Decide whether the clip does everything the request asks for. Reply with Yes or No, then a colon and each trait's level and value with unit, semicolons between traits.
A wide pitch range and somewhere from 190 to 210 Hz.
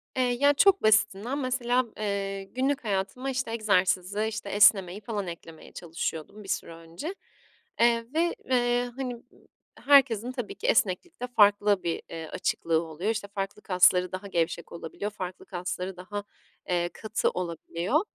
No: average, 5.0 semitones; high, 205 Hz